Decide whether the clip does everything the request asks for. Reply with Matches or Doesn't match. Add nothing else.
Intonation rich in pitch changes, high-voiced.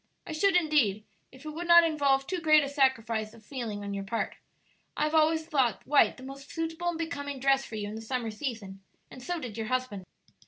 Matches